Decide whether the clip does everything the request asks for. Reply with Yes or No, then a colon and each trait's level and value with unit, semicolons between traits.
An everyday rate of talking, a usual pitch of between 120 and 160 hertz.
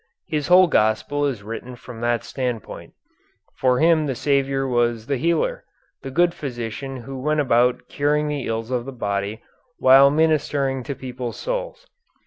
Yes: average, 155 wpm; low, 135 Hz